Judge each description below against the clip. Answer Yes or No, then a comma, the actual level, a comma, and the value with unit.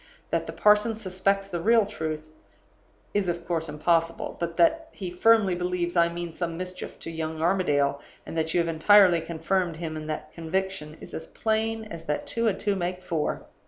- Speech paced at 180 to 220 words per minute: Yes, average, 190 wpm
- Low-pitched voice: No, medium, 175 Hz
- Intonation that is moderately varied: Yes, average, 3.1 semitones